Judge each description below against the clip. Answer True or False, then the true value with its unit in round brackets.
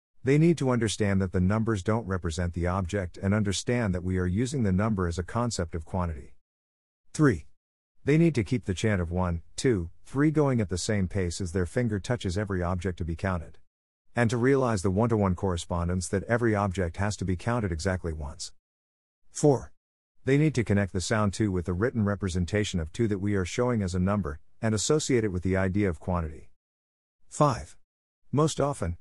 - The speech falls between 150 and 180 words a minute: False (205 wpm)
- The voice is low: True (95 Hz)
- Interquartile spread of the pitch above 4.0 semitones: True (4.4 semitones)